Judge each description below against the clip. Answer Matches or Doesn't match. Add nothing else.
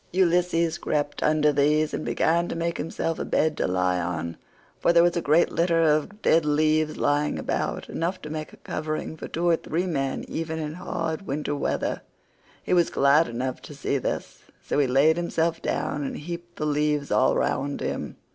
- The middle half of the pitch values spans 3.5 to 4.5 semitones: Doesn't match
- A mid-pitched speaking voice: Matches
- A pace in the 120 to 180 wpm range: Doesn't match